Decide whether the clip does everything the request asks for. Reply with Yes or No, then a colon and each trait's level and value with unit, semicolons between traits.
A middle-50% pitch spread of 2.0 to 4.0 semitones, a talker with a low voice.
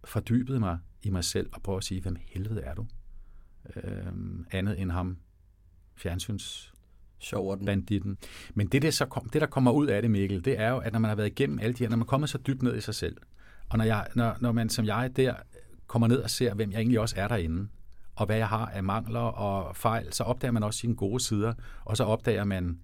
Yes: average, 3.6 semitones; low, 110 Hz